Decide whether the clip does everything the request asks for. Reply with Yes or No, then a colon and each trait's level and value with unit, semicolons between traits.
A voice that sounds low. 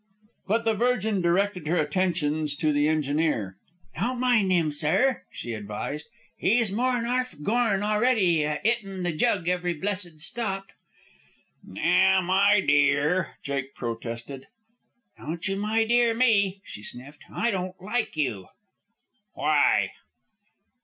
No: medium, 185 Hz